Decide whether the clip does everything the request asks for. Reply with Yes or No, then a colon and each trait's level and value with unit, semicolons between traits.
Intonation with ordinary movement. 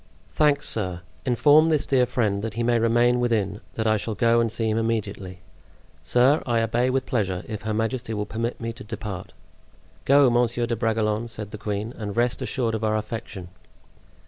No: narrow, 2.2 semitones